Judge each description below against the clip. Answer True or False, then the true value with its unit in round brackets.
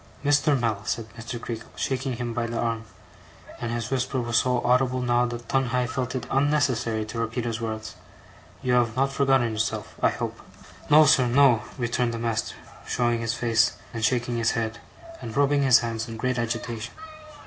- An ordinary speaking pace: True (180 wpm)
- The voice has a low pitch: True (120 Hz)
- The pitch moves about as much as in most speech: False (1.9 semitones)